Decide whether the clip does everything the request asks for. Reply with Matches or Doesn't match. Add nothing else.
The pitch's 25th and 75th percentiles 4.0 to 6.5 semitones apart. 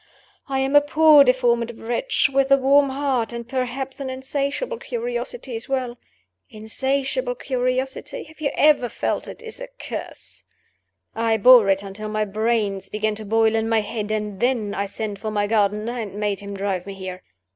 Matches